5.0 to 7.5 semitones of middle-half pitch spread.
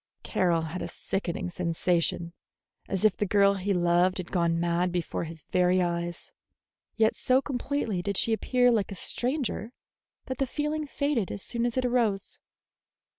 Yes: wide, 5.6 semitones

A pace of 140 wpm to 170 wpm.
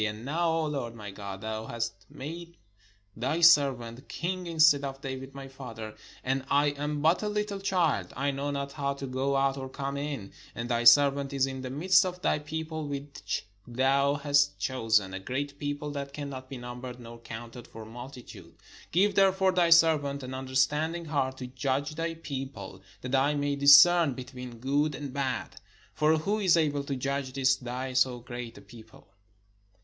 No: average, 185 wpm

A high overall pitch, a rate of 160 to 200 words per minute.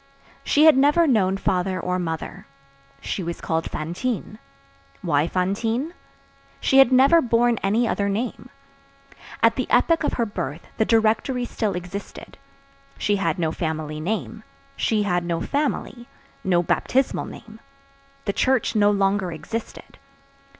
No: high, 205 Hz; slow, 135 wpm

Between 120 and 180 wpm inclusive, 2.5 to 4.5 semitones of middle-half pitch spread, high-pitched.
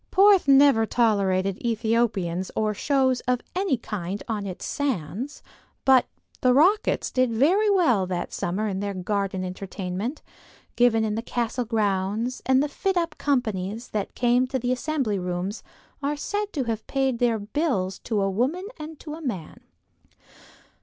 No: average, 160 wpm; wide, 5.6 semitones; high, 235 Hz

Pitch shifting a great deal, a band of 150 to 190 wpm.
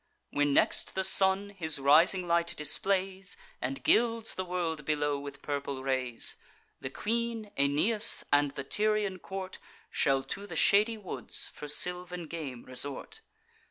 No: wide, 5.7 semitones; average, 140 wpm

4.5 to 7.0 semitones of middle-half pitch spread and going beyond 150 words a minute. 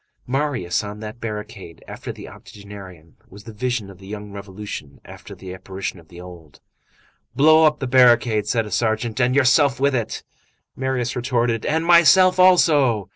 Yes: average, 4.9 semitones; average, 165 wpm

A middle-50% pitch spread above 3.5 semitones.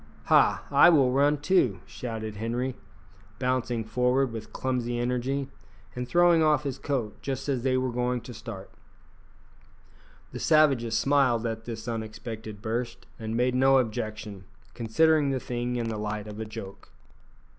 No: average, 3.2 semitones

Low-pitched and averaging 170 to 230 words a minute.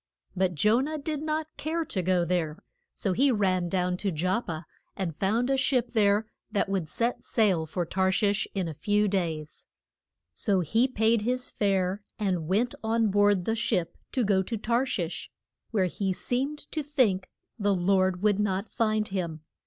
No: high, 200 Hz; average, 180 wpm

